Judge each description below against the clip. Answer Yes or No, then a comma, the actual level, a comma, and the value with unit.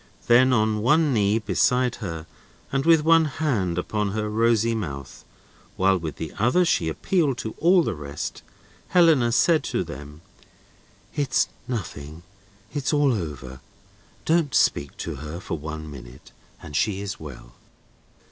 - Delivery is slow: No, average, 145 wpm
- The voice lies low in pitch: Yes, low, 105 Hz